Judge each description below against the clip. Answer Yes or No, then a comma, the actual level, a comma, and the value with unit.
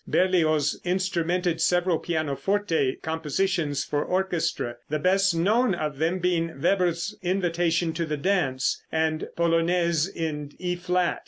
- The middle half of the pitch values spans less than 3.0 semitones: Yes, narrow, 2.5 semitones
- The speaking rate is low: Yes, slow, 120 wpm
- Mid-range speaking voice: Yes, medium, 170 Hz